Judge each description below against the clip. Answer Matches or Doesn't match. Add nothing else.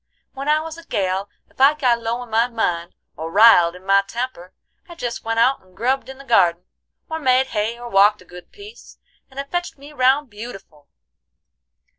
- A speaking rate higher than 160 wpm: Matches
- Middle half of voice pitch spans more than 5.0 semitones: Matches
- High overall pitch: Matches